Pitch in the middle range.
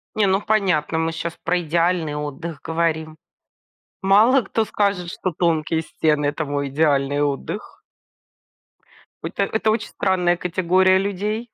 Yes: medium, 170 Hz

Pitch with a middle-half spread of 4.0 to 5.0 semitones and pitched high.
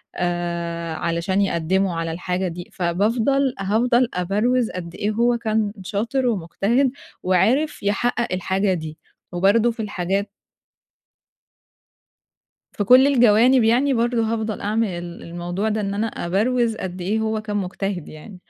Yes: average, 4.4 semitones; high, 205 Hz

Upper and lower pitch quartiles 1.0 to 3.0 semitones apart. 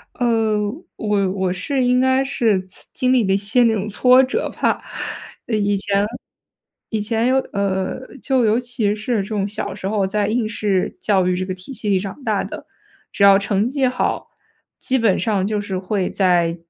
No: average, 3.8 semitones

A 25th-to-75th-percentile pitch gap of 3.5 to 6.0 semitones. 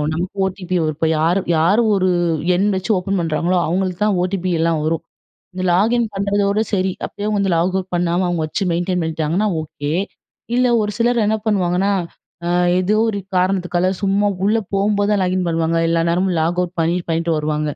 No: average, 2.9 semitones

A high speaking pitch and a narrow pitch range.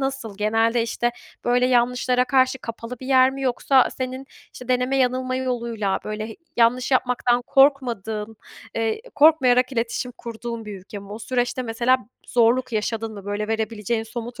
Yes: high, 240 Hz; narrow, 2.3 semitones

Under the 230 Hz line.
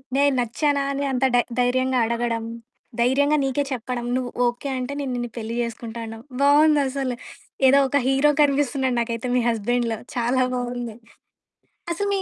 No: very high, 250 Hz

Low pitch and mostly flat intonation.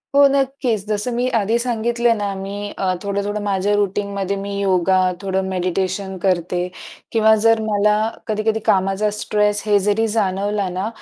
No: high, 205 Hz; narrow, 2.1 semitones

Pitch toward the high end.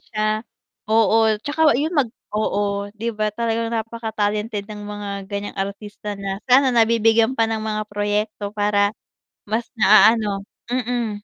Yes: high, 215 Hz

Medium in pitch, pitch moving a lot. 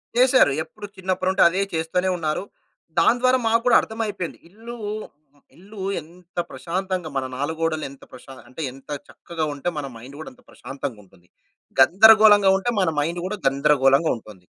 Yes: medium, 170 Hz; wide, 6.3 semitones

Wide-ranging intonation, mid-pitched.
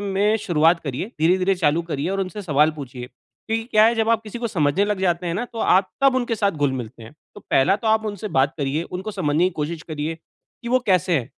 Yes: wide, 6.0 semitones; medium, 180 Hz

